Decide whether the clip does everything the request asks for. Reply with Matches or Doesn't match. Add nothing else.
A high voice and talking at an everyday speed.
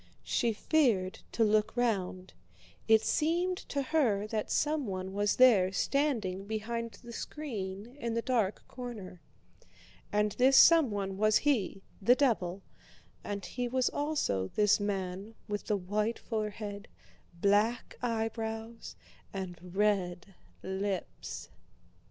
Doesn't match